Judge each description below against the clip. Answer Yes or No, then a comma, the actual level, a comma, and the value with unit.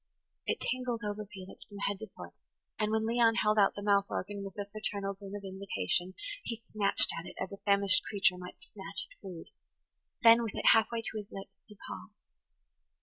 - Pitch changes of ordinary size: No, narrow, 1.8 semitones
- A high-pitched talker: Yes, high, 200 Hz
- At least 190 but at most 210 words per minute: Yes, fast, 205 wpm